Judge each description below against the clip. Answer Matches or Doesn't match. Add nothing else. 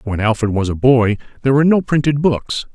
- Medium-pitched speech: Doesn't match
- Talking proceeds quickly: Matches